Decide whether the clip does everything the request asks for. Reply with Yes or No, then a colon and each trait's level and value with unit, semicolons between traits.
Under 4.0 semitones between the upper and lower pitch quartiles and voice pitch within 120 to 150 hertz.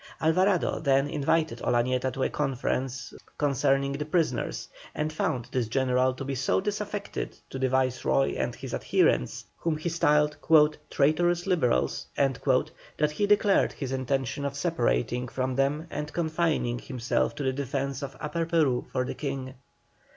Yes: average, 3.3 semitones; medium, 140 Hz